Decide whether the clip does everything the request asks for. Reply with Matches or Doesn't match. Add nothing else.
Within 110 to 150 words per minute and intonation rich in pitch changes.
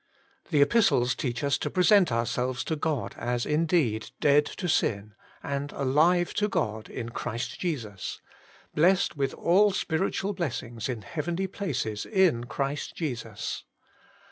Matches